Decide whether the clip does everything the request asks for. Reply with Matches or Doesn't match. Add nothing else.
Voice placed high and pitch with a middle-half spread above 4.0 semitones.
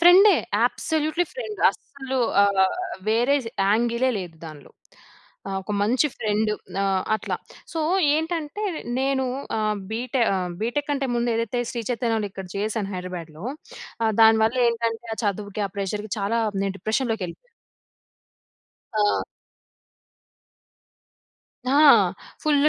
Matches